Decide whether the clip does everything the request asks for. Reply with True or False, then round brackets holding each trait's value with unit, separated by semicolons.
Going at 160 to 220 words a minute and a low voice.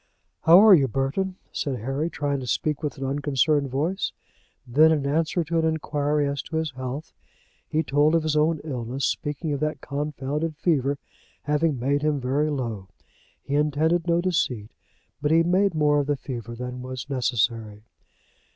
False (170 wpm; 145 Hz)